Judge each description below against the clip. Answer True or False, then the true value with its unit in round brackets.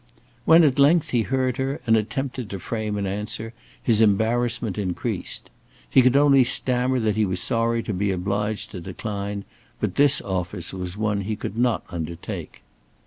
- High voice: False (110 Hz)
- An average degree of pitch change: True (3.9 semitones)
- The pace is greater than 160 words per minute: True (170 wpm)